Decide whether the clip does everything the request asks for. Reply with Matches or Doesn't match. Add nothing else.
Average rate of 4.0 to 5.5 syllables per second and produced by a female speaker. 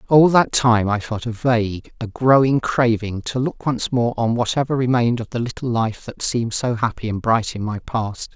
Doesn't match